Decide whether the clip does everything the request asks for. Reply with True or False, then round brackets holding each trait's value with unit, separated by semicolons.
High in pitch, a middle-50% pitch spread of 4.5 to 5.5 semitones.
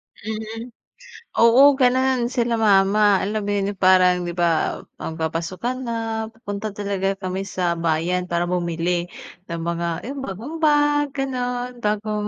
True (205 Hz; 5.2 semitones)